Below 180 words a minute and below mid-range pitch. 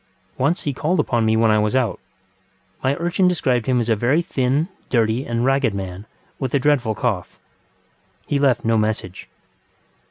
Yes: average, 170 wpm; low, 125 Hz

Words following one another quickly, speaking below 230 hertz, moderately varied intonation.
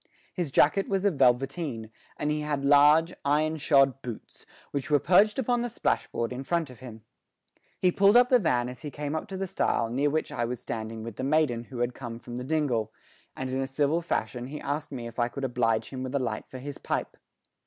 Yes: fast, 230 wpm; medium, 140 Hz; average, 4.3 semitones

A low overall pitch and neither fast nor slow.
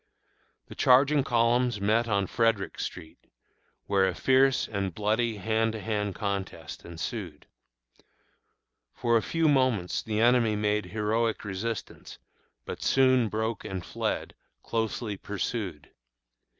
No: low, 110 Hz; slow, 120 wpm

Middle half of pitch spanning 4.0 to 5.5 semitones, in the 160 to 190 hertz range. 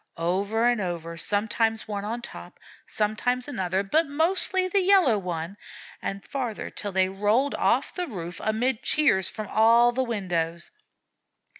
No: average, 4.7 semitones; high, 215 Hz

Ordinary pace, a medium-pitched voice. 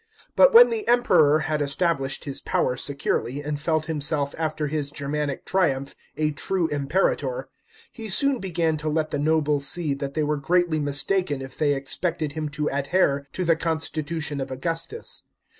Yes: average, 170 wpm; medium, 155 Hz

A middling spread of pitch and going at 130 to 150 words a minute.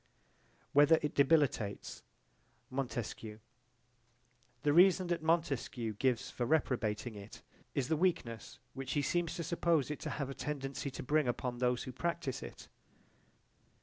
Yes: average, 4.6 semitones; average, 140 wpm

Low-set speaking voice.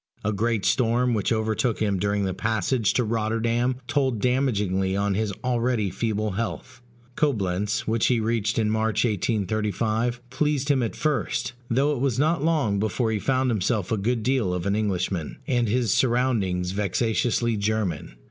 Yes: low, 110 Hz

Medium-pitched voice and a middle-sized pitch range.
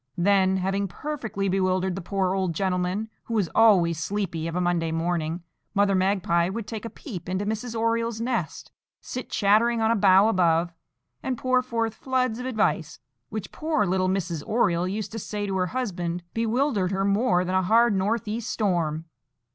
No: high, 195 Hz; average, 3.9 semitones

